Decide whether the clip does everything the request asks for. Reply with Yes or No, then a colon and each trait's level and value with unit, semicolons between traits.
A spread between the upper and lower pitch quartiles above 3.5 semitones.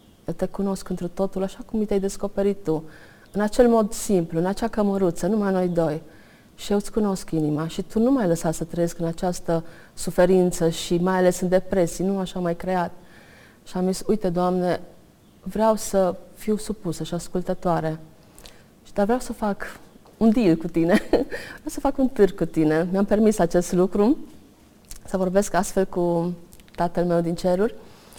No: average, 2.9 semitones